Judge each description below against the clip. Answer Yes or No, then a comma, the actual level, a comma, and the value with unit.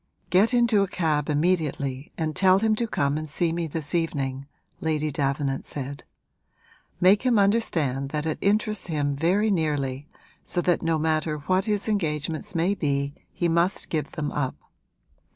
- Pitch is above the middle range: No, medium, 160 Hz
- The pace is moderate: Yes, average, 160 wpm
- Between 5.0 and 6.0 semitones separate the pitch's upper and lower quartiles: No, average, 4.4 semitones